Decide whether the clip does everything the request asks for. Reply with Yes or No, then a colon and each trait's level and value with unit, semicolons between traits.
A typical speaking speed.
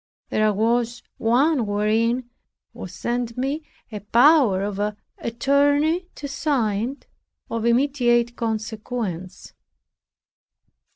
No: slow, 90 wpm